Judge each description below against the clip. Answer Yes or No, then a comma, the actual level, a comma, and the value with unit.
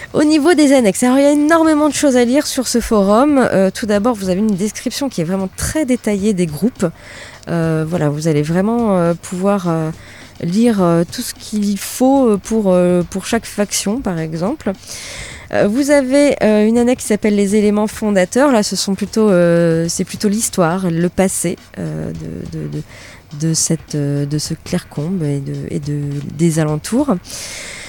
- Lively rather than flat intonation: Yes, wide, 5.9 semitones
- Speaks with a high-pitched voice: Yes, high, 195 Hz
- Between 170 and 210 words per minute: Yes, average, 185 wpm